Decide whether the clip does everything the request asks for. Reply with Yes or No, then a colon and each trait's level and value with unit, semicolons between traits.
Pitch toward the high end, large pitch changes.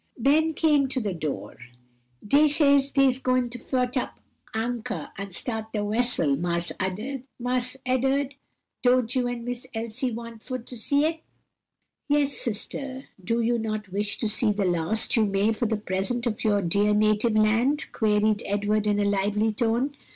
No: high, 230 Hz; average, 3.5 semitones